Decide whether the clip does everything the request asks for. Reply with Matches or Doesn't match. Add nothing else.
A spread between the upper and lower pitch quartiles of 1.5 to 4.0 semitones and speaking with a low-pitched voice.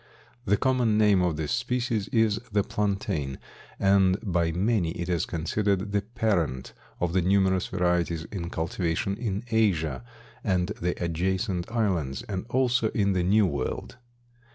Matches